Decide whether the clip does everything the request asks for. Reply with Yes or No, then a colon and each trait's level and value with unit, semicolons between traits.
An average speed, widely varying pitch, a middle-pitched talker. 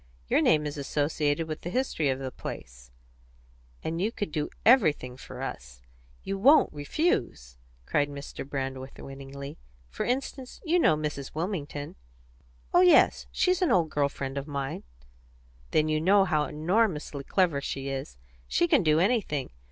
Yes: average, 155 wpm; wide, 5.9 semitones; medium, 150 Hz